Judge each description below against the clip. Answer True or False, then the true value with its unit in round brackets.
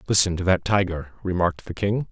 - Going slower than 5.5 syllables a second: False (6.1 syllables/s)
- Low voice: True (95 Hz)